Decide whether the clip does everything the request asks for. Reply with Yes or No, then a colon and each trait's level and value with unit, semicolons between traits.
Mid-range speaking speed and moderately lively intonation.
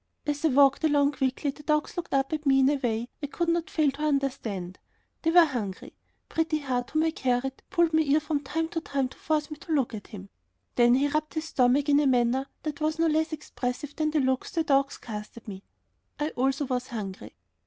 No: fast, 230 wpm; average, 3.5 semitones